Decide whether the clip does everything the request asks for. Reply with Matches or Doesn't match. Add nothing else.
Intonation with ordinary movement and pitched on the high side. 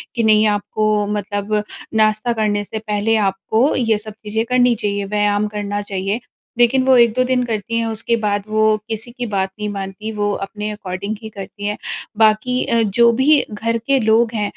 Doesn't match